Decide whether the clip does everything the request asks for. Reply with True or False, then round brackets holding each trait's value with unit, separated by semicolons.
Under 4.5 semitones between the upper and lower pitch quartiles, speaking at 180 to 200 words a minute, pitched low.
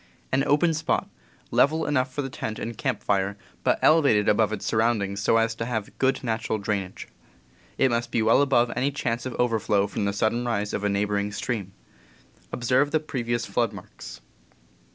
True (3.9 semitones; 185 wpm; 115 Hz)